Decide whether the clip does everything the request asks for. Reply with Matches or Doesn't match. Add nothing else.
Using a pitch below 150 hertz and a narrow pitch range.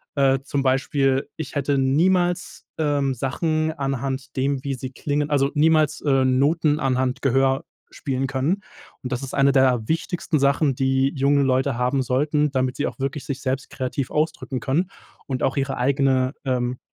Matches